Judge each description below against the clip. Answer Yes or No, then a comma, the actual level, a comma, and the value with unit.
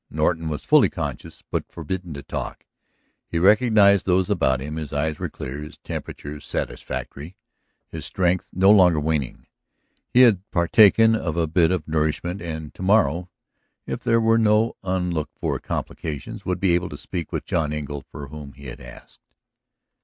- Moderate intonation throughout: Yes, average, 3.9 semitones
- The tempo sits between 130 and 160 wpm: No, average, 170 wpm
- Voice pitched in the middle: No, very low, 85 Hz